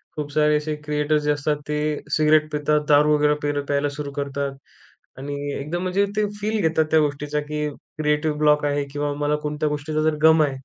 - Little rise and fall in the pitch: Yes, narrow, 0.9 semitones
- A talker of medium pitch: Yes, medium, 150 Hz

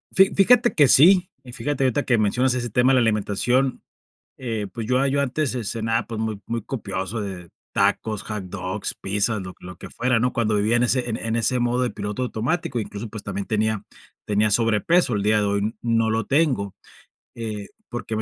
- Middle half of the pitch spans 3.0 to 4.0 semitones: Yes, average, 3.4 semitones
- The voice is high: No, low, 115 Hz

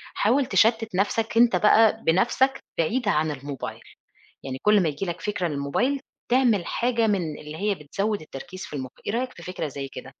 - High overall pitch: Yes, high, 200 Hz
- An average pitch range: No, wide, 7.0 semitones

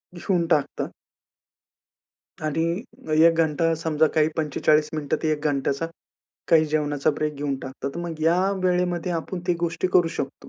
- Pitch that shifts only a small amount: Yes, narrow, 2.1 semitones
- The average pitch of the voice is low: No, medium, 160 Hz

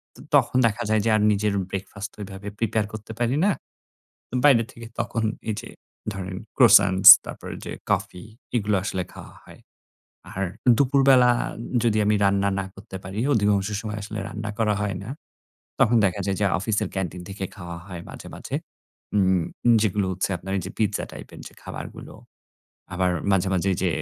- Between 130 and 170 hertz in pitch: No, low, 100 Hz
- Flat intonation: Yes, narrow, 2.3 semitones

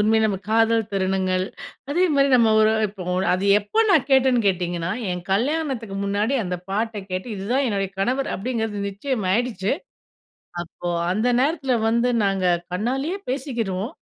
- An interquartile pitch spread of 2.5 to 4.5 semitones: No, average, 5.0 semitones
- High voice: Yes, high, 220 Hz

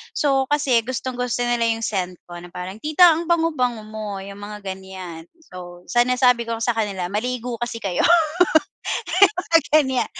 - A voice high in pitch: Yes, high, 230 Hz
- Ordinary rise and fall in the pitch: Yes, average, 4.7 semitones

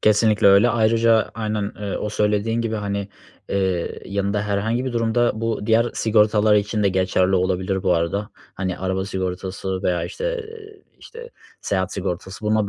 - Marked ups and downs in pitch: No, average, 2.8 semitones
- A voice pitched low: Yes, low, 105 Hz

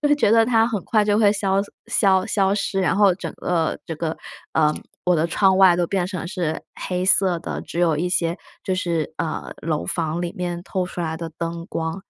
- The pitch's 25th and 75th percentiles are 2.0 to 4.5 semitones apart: Yes, average, 2.7 semitones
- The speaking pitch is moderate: Yes, medium, 180 Hz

